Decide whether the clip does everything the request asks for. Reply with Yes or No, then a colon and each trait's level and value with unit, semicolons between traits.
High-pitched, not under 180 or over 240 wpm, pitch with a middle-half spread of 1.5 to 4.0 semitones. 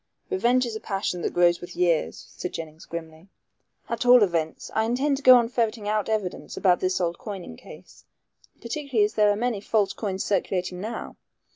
No: high, 205 Hz; average, 185 wpm; average, 4.7 semitones